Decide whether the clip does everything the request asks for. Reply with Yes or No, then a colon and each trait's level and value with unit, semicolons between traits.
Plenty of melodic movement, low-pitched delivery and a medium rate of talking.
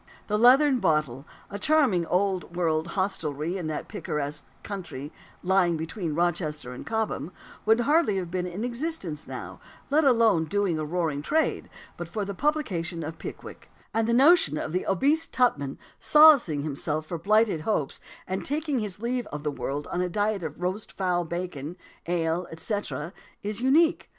No: wide, 6.1 semitones; medium, 180 Hz; average, 165 wpm